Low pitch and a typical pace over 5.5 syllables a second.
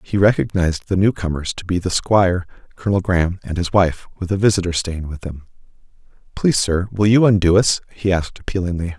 Yes: very low, 90 Hz; 6.1 syllables/s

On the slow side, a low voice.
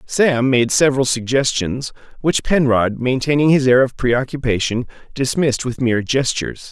Yes: slow, 115 wpm; low, 130 Hz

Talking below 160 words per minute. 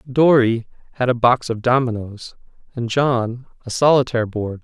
Yes: average, 140 wpm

